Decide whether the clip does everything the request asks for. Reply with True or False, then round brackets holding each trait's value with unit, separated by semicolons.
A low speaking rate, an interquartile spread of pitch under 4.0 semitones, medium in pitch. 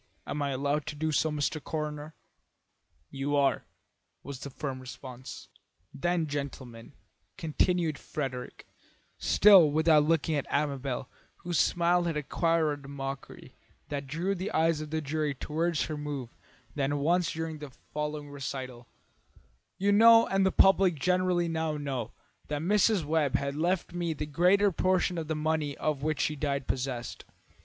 False (150 wpm; 3.1 semitones; 150 Hz)